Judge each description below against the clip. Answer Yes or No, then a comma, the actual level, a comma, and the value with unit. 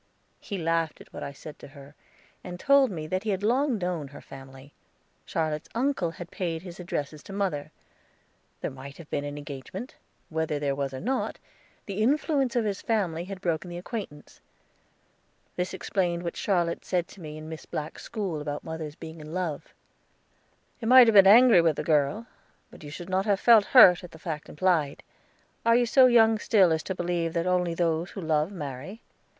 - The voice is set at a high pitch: No, medium, 175 Hz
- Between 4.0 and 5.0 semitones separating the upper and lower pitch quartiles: Yes, average, 4.7 semitones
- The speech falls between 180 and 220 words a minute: Yes, average, 195 wpm